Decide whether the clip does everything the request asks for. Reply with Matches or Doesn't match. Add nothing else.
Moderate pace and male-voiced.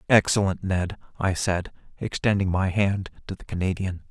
Matches